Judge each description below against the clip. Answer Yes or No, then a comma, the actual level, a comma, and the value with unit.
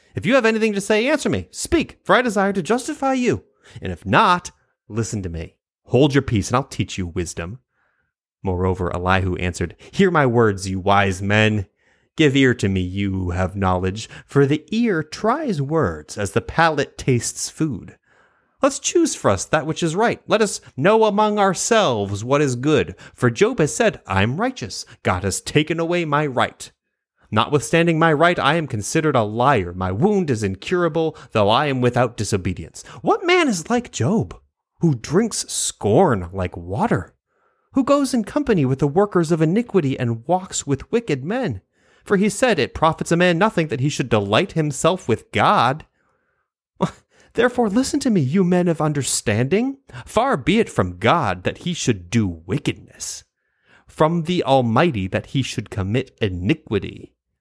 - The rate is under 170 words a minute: No, average, 175 wpm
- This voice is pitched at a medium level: Yes, medium, 150 Hz